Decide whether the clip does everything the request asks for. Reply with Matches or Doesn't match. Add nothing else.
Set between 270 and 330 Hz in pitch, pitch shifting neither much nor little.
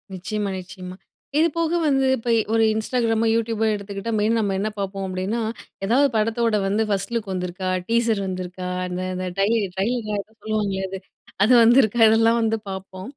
Doesn't match